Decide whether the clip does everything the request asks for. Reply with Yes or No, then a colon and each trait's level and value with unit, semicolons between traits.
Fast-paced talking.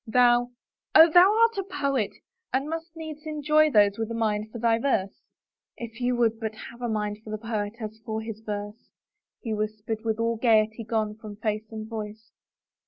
Yes: fast, 210 wpm